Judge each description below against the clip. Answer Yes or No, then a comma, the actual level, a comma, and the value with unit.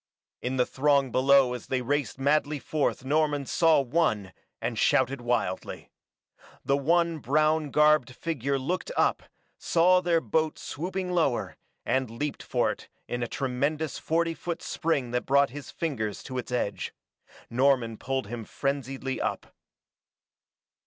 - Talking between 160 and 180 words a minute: No, average, 140 wpm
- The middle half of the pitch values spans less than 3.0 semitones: No, average, 3.7 semitones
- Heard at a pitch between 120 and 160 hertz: Yes, medium, 140 Hz